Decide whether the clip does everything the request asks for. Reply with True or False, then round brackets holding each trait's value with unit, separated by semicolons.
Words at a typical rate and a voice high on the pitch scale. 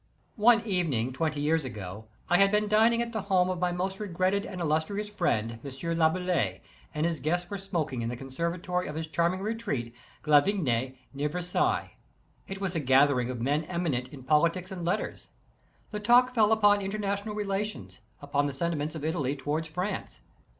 False (180 wpm; 170 Hz)